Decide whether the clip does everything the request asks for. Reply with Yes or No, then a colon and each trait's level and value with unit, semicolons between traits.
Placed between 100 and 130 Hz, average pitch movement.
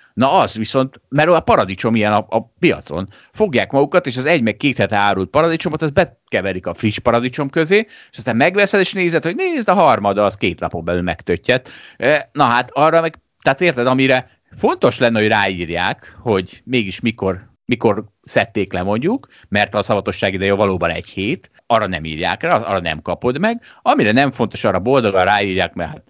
No: low, 120 Hz; wide, 7.7 semitones